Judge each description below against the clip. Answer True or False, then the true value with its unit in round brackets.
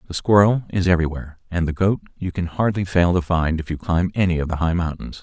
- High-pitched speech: False (90 Hz)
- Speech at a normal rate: False (240 wpm)